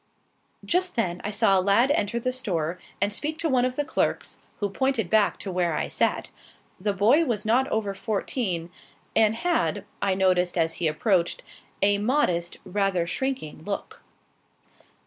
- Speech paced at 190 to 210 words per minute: No, average, 165 wpm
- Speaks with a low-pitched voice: No, high, 205 Hz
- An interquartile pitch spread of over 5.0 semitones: Yes, wide, 5.6 semitones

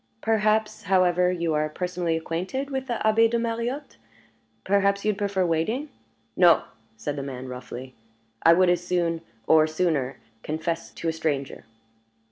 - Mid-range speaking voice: Yes, medium, 175 Hz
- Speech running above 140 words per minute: Yes, average, 155 wpm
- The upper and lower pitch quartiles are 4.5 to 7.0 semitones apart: Yes, average, 5.1 semitones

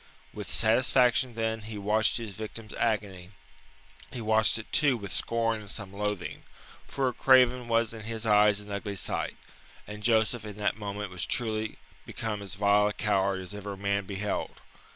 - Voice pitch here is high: No, low, 105 Hz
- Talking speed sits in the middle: Yes, average, 175 wpm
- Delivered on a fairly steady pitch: Yes, narrow, 2.0 semitones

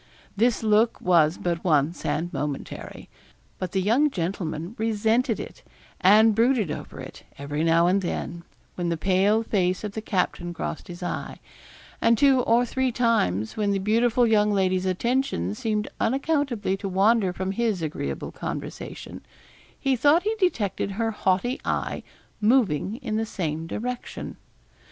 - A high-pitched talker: Yes, high, 205 Hz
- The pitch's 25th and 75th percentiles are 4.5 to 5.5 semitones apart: Yes, average, 4.8 semitones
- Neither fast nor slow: Yes, average, 150 wpm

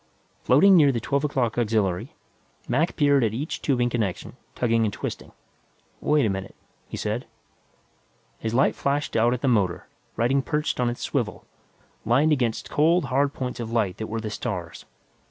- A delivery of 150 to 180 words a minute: Yes, average, 170 wpm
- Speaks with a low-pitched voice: Yes, low, 120 Hz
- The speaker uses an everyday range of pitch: Yes, average, 4.1 semitones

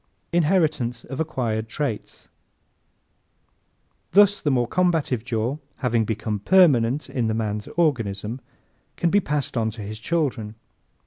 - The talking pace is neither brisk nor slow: No, slow, 130 wpm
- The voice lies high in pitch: No, low, 125 Hz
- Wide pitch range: Yes, wide, 5.9 semitones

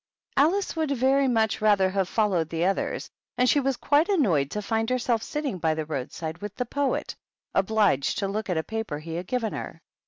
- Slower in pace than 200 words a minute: No, fast, 205 wpm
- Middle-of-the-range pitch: No, high, 215 Hz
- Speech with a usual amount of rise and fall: No, wide, 6.5 semitones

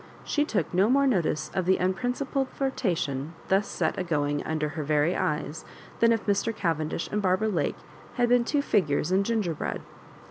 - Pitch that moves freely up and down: Yes, wide, 6.6 semitones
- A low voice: No, medium, 185 Hz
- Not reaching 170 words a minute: No, average, 175 wpm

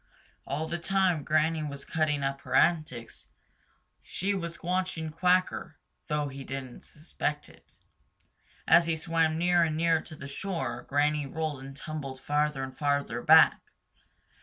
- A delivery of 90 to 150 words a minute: Yes, average, 145 wpm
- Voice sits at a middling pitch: Yes, medium, 155 Hz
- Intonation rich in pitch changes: No, average, 3.0 semitones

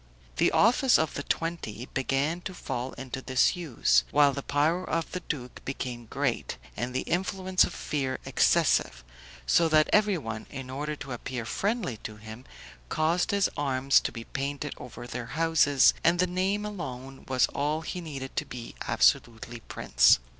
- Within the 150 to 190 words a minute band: Yes, average, 160 wpm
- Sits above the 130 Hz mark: Yes, medium, 140 Hz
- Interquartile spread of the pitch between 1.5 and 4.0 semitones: No, average, 5.1 semitones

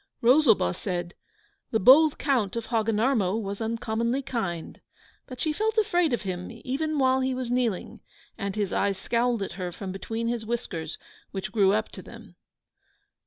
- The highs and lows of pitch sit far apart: No, average, 4.7 semitones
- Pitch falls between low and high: No, high, 230 Hz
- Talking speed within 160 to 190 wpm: Yes, average, 165 wpm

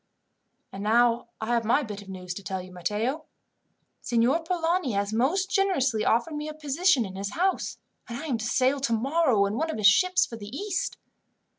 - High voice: Yes, high, 240 Hz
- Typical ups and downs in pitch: No, wide, 7.3 semitones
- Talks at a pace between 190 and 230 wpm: Yes, average, 195 wpm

